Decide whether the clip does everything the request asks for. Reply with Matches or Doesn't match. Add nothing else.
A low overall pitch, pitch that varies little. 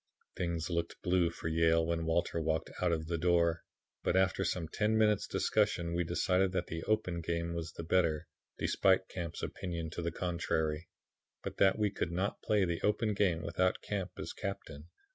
Matches